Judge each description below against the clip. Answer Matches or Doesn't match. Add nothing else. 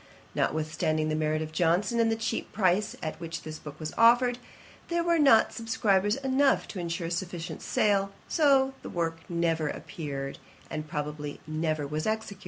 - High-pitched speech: Doesn't match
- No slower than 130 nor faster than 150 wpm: Doesn't match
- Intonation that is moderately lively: Doesn't match